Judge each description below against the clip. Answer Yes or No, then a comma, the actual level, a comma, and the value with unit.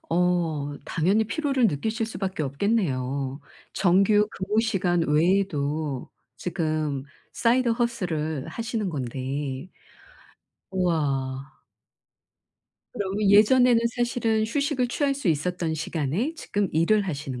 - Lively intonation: Yes, wide, 6.9 semitones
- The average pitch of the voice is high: No, medium, 180 Hz